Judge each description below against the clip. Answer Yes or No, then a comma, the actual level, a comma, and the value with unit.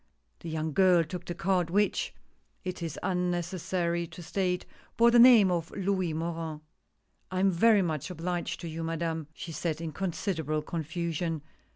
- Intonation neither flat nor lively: No, narrow, 2.2 semitones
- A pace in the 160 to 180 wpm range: Yes, average, 165 wpm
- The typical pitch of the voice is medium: Yes, medium, 170 Hz